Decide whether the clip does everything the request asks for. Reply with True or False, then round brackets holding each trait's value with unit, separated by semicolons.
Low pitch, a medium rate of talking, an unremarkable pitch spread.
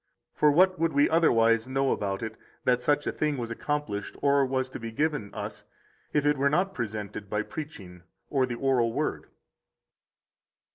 True (130 Hz; 175 wpm; 4.6 semitones)